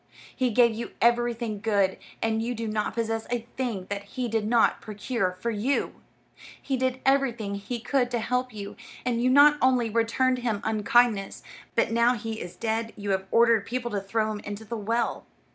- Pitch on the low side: No, high, 230 Hz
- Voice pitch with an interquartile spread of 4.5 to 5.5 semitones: No, narrow, 2.5 semitones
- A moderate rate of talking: Yes, average, 190 wpm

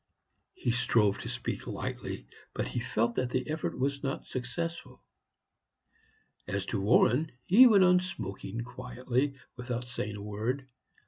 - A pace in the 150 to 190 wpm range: No, average, 140 wpm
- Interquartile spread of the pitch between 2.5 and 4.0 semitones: Yes, average, 3.7 semitones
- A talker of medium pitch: No, low, 125 Hz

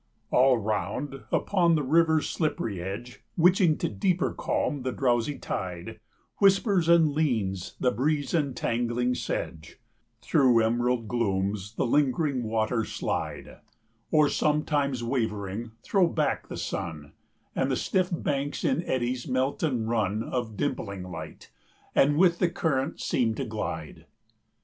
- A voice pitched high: No, low, 125 Hz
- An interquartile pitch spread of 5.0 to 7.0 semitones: Yes, wide, 5.4 semitones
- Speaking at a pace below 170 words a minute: Yes, slow, 135 wpm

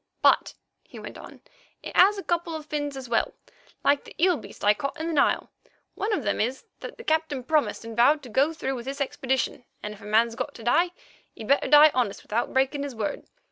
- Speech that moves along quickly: Yes, fast, 230 wpm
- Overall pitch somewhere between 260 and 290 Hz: Yes, very high, 275 Hz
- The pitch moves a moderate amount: Yes, average, 4.7 semitones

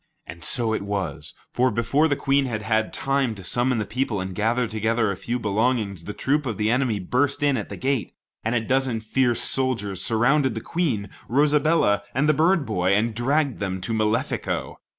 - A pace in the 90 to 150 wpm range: No, average, 195 wpm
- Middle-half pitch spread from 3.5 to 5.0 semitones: Yes, average, 4.0 semitones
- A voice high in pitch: No, low, 115 Hz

